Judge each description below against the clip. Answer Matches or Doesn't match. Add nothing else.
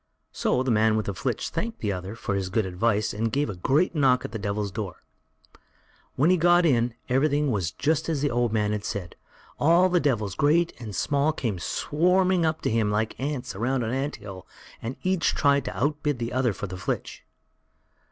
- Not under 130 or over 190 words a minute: Doesn't match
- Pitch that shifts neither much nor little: Doesn't match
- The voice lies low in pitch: Matches